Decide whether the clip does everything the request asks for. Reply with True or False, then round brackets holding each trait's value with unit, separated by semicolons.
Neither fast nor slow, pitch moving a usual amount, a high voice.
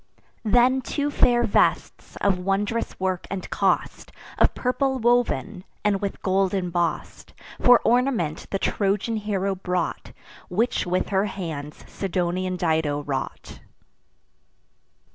False (115 wpm; 4.3 semitones; 195 Hz)